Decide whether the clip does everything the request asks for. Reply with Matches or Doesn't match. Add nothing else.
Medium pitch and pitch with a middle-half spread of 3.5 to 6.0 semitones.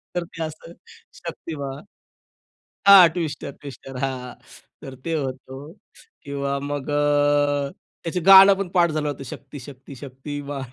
Doesn't match